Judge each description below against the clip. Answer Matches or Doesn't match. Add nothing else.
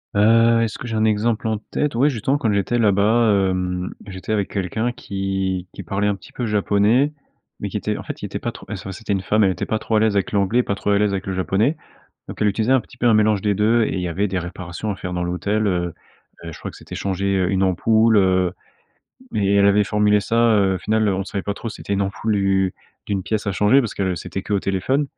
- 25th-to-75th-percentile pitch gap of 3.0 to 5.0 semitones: Doesn't match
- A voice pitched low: Matches